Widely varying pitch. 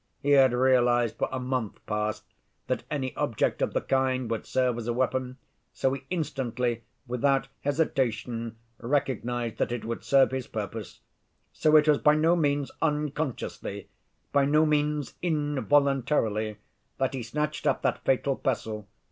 No: average, 3.4 semitones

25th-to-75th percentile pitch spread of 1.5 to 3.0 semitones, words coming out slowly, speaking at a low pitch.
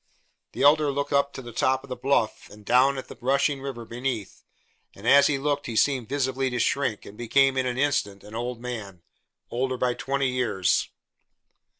No: average, 2.7 semitones; average, 195 wpm; low, 130 Hz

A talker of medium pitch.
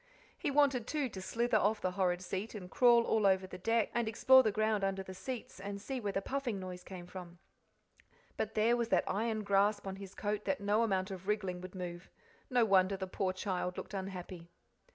No: high, 200 Hz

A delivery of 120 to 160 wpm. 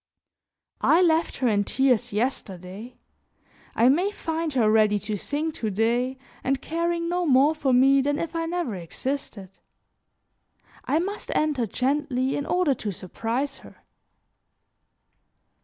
Yes: slow, 135 wpm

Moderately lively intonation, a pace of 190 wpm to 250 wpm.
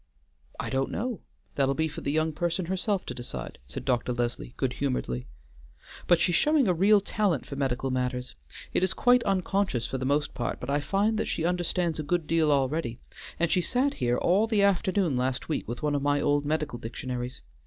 No: wide, 6.3 semitones; fast, 205 wpm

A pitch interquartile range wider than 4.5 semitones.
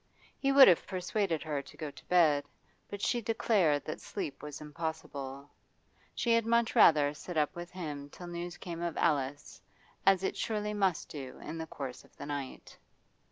Yes: average, 4.9 semitones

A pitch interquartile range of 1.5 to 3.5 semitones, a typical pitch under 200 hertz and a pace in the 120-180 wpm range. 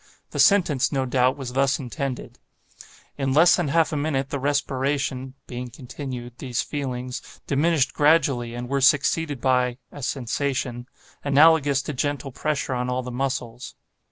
Yes: narrow, 2.4 semitones; low, 135 Hz; average, 150 wpm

